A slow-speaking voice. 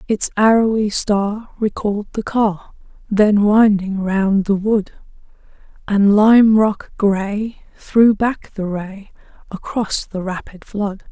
Yes: slow, 125 wpm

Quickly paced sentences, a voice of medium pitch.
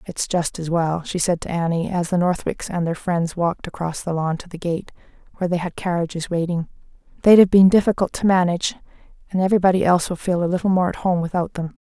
Yes: fast, 225 wpm; medium, 175 Hz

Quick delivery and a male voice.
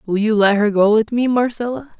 No: fast, 240 wpm; female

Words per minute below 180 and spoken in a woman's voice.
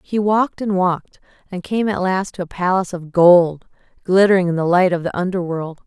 No: fast, 205 wpm; female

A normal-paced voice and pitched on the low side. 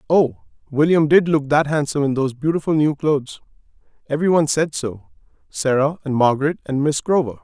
No: average, 155 wpm; medium, 145 Hz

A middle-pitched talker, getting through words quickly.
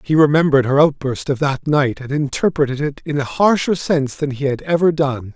Yes: medium, 145 Hz; fast, 215 wpm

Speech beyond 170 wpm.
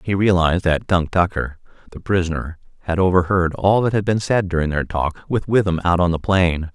Yes: fast, 205 wpm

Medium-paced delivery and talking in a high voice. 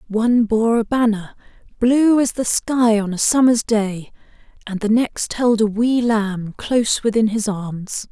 Yes: average, 170 wpm; high, 225 Hz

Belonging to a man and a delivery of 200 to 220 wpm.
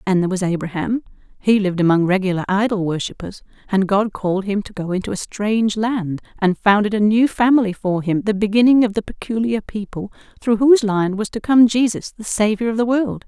No: female; fast, 205 wpm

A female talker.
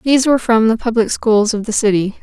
Yes: female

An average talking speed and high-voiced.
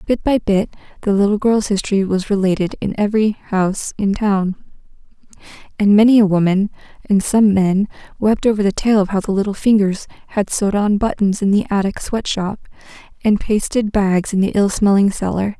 Yes: average, 175 wpm; high, 205 Hz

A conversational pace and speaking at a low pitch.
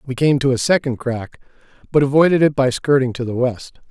No: fast, 215 wpm; low, 130 Hz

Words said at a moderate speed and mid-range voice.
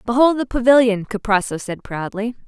No: average, 145 wpm; high, 225 Hz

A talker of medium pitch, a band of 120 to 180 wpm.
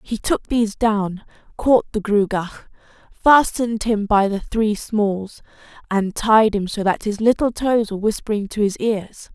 No: high, 215 Hz; average, 165 wpm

